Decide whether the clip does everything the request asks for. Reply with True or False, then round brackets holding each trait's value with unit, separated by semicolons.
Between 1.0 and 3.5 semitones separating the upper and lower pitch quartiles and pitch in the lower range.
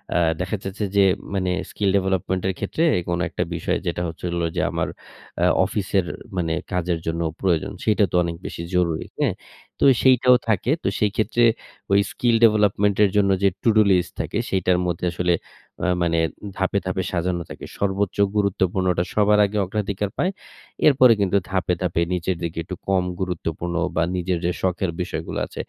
True (2.6 semitones; 95 Hz)